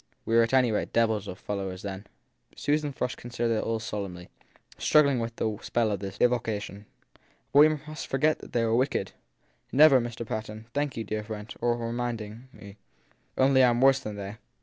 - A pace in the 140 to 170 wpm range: No, average, 195 wpm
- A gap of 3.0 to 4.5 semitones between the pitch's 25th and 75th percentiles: Yes, average, 3.6 semitones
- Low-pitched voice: Yes, low, 115 Hz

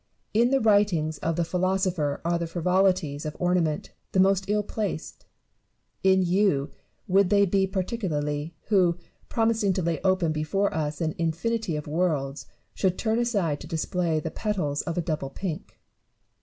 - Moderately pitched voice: Yes, medium, 180 Hz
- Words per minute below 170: Yes, average, 155 wpm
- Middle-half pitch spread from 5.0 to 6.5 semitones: No, average, 4.0 semitones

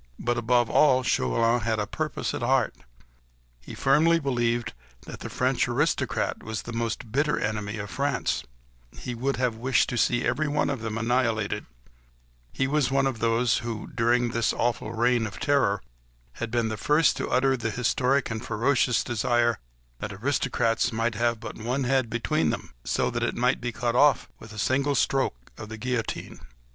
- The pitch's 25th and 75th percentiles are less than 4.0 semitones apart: Yes, average, 2.8 semitones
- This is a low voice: Yes, low, 120 Hz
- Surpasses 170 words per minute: Yes, average, 180 wpm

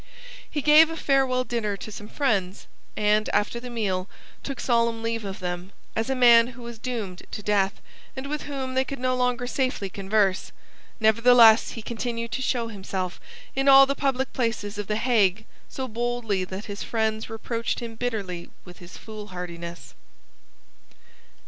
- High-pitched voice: Yes, high, 230 Hz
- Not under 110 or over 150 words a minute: No, average, 165 wpm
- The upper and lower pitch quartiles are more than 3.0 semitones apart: Yes, average, 3.7 semitones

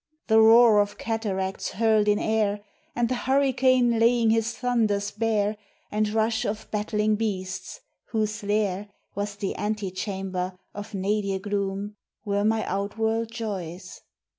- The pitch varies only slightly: Yes, narrow, 1.9 semitones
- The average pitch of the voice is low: No, high, 210 Hz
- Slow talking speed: Yes, slow, 130 wpm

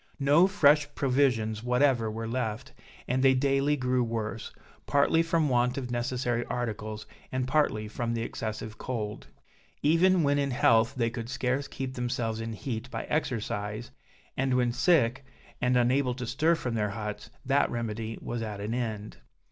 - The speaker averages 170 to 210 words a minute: No, average, 160 wpm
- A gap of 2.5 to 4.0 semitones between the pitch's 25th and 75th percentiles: Yes, average, 3.3 semitones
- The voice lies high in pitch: No, low, 125 Hz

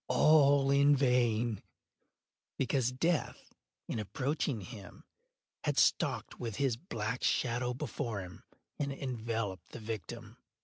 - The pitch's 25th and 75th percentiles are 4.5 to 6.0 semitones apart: No, average, 3.7 semitones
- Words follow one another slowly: Yes, slow, 115 wpm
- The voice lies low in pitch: Yes, low, 125 Hz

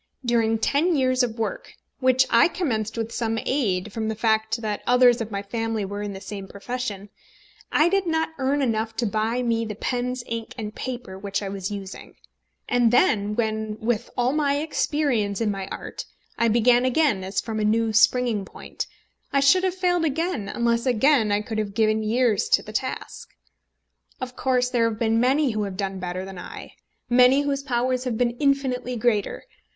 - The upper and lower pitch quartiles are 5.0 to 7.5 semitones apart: No, average, 3.2 semitones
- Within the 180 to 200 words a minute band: Yes, average, 190 wpm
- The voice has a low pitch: No, high, 230 Hz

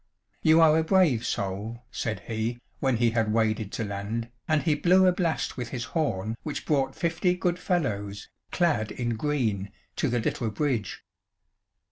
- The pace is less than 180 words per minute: Yes, average, 165 wpm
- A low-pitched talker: Yes, low, 120 Hz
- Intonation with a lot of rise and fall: Yes, wide, 6.4 semitones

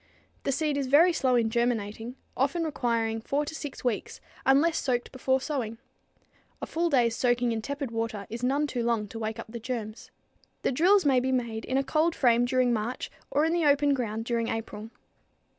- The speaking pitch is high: Yes, very high, 250 Hz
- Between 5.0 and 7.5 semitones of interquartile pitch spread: No, average, 3.8 semitones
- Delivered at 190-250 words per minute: Yes, average, 195 wpm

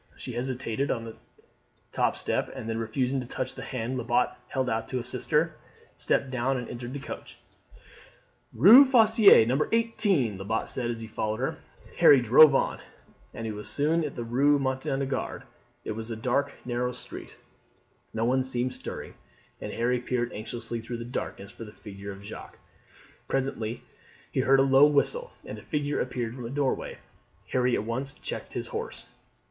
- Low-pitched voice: Yes, low, 125 Hz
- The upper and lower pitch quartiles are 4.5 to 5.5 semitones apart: No, average, 3.1 semitones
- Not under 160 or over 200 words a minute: Yes, average, 175 wpm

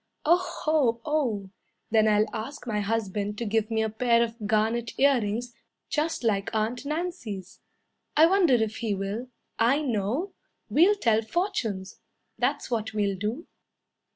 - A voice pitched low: No, high, 230 Hz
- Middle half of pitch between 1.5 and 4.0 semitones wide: No, average, 4.9 semitones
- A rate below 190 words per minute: Yes, average, 145 wpm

